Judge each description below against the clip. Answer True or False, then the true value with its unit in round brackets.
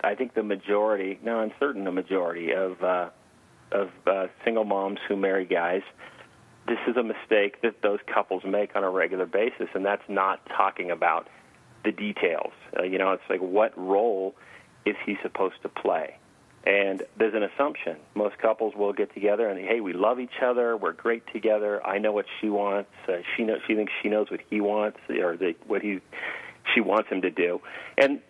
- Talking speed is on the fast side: False (195 wpm)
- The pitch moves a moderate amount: False (2.0 semitones)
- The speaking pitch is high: False (105 Hz)